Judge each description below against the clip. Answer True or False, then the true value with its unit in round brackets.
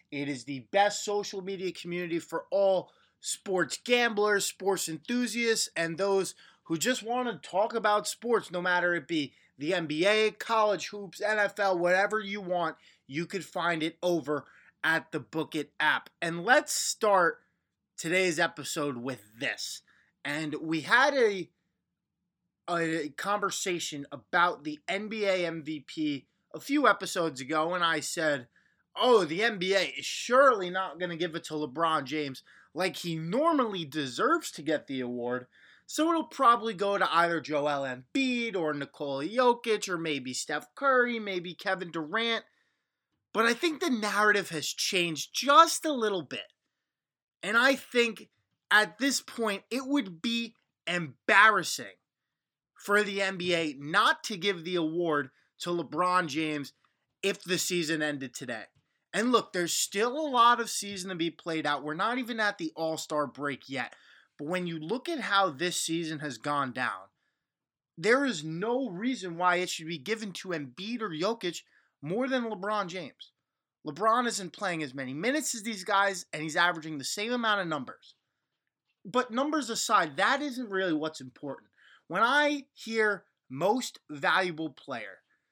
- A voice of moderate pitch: True (180 Hz)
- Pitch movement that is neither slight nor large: False (5.7 semitones)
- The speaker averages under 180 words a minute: True (155 wpm)